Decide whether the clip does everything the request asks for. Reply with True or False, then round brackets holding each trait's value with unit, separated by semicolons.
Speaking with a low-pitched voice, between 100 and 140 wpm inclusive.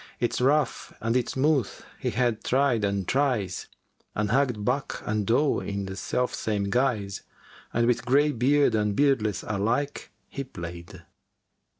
False (120 Hz; 150 wpm)